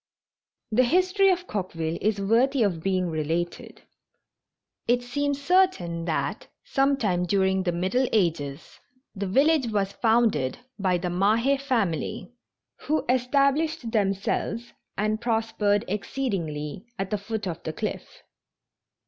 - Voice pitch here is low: No, high, 210 Hz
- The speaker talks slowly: Yes, slow, 125 wpm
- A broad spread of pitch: Yes, wide, 6.0 semitones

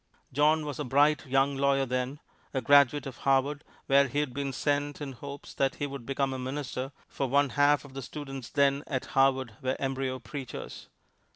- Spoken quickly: No, average, 185 wpm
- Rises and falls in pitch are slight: Yes, narrow, 1.4 semitones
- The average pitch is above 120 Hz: Yes, low, 135 Hz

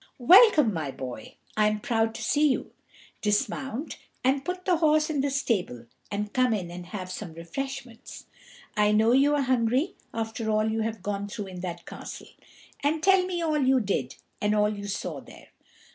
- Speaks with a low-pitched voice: No, high, 225 Hz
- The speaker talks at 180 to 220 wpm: Yes, average, 185 wpm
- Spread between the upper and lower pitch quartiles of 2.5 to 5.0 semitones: No, wide, 5.5 semitones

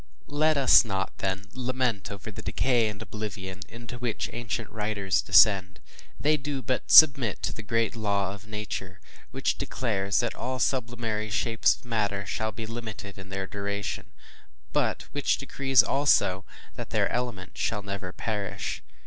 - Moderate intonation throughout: Yes, average, 3.6 semitones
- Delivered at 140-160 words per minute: Yes, average, 155 wpm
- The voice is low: Yes, low, 110 Hz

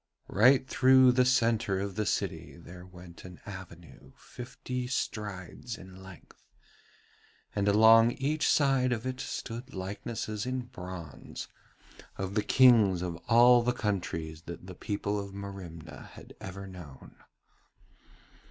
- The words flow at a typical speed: No, slow, 130 wpm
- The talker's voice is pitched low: Yes, low, 100 Hz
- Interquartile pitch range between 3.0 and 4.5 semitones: No, average, 5.0 semitones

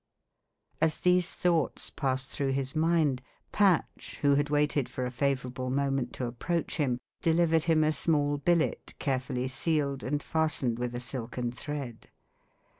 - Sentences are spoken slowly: No, average, 145 wpm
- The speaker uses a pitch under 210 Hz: Yes, medium, 140 Hz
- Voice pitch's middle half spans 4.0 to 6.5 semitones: No, average, 3.6 semitones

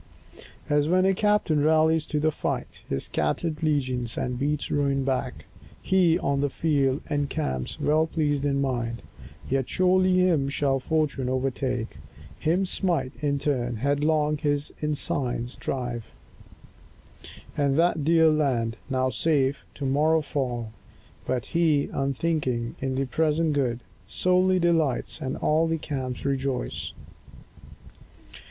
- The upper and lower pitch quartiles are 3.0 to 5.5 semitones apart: Yes, average, 3.4 semitones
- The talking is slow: Yes, slow, 130 wpm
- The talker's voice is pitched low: No, medium, 145 Hz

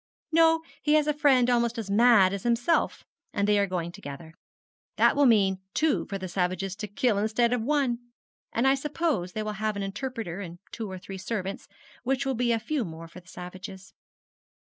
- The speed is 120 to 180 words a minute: No, average, 200 wpm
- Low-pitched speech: No, high, 215 Hz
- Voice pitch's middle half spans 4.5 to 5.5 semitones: Yes, average, 5.1 semitones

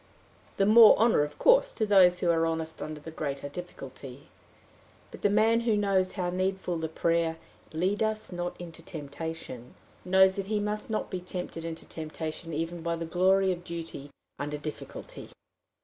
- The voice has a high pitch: No, medium, 175 Hz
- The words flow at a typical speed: Yes, average, 170 wpm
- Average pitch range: Yes, average, 3.2 semitones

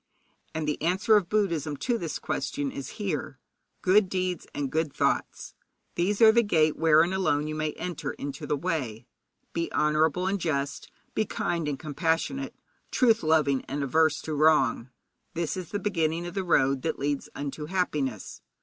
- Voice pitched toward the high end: No, medium, 160 Hz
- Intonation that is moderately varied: Yes, average, 4.0 semitones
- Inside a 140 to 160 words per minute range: No, average, 170 wpm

